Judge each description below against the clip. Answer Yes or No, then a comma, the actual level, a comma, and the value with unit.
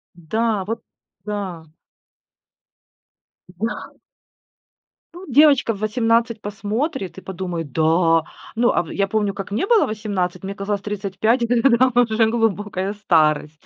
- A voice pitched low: No, high, 205 Hz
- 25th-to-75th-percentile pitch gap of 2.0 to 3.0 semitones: No, average, 3.7 semitones